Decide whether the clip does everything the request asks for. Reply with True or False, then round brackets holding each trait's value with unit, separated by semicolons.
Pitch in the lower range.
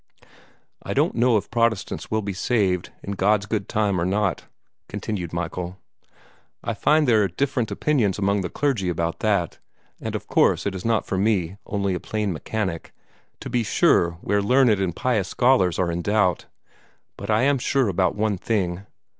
True (100 Hz)